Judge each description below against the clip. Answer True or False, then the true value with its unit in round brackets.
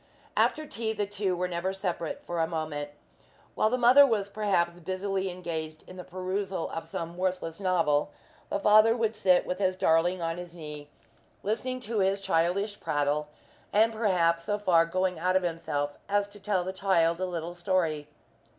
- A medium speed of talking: True (180 wpm)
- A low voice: False (185 Hz)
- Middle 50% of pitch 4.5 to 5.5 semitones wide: False (3.3 semitones)